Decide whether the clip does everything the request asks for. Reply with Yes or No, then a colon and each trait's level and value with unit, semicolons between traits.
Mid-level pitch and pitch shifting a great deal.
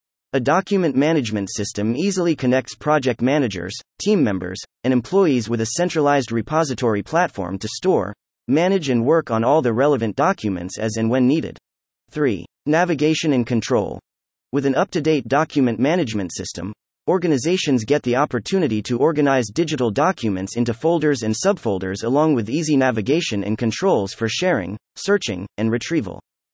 No: low, 125 Hz; wide, 6.3 semitones